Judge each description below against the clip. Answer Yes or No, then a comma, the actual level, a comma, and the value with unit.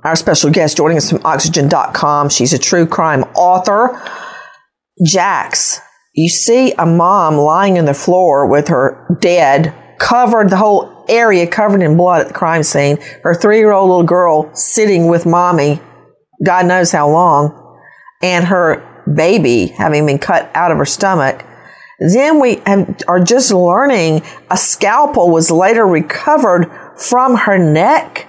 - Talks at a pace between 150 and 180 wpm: Yes, average, 155 wpm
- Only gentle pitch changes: No, average, 4.0 semitones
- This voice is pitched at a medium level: Yes, medium, 175 Hz